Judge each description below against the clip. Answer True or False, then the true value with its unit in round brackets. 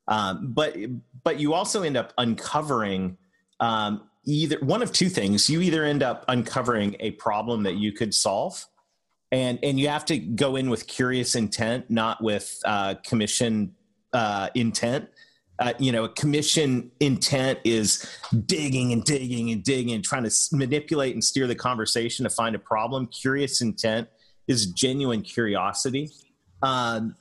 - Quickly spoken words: False (155 wpm)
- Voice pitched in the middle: False (125 Hz)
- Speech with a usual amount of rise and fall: True (3.9 semitones)